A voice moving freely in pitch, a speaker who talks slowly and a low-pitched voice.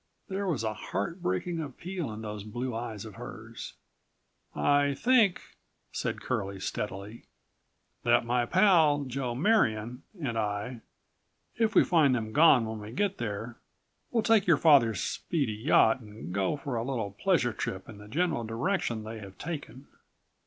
No: wide, 6.5 semitones; average, 150 wpm; low, 120 Hz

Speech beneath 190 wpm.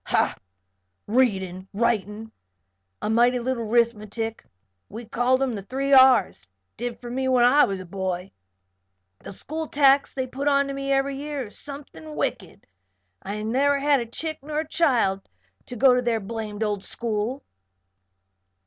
Yes: average, 155 wpm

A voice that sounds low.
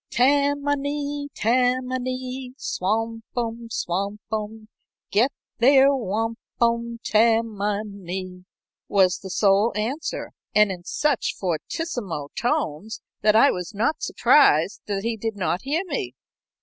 No: high, 225 Hz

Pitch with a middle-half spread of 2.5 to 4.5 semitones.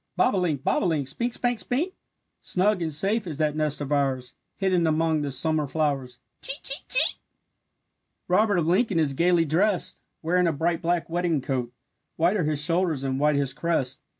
Yes: average, 3.9 semitones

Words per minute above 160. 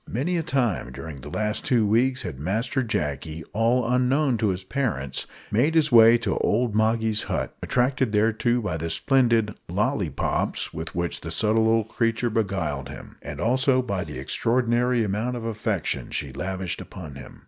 Yes: average, 170 wpm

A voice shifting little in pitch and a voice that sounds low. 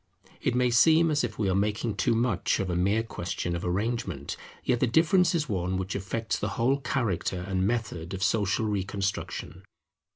No: average, 4.4 semitones; low, 105 Hz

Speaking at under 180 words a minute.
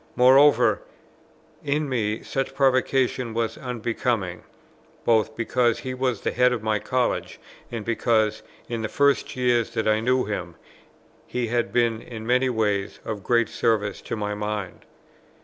Yes: average, 150 wpm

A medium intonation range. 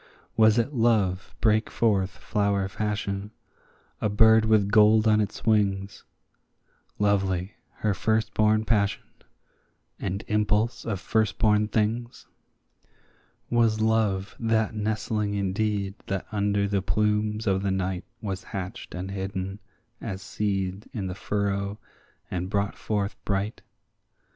No: narrow, 1.9 semitones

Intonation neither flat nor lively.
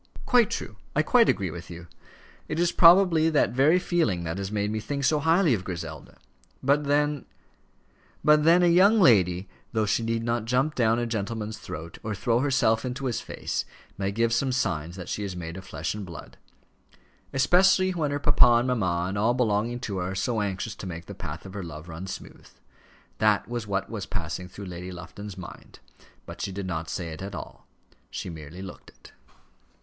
No: wide, 7.0 semitones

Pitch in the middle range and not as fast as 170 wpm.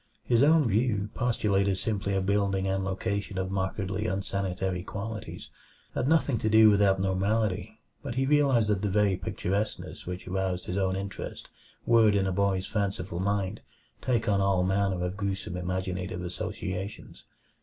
No: low, 100 Hz; average, 155 wpm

